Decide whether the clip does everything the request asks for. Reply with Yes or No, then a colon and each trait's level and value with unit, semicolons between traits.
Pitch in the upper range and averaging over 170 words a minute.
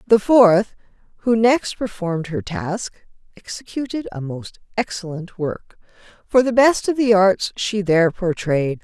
No: high, 200 Hz; average, 145 wpm